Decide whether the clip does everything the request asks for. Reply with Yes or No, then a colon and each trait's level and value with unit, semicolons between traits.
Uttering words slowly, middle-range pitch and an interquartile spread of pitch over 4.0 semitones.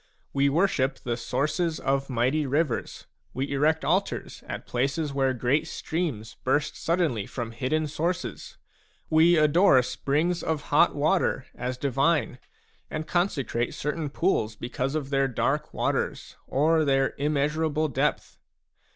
No: slow, 130 wpm; medium, 145 Hz; average, 3.3 semitones